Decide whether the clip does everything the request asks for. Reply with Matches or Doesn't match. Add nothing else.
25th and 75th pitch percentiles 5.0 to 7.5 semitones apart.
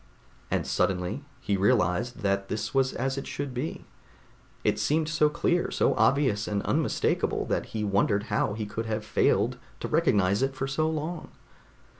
Matches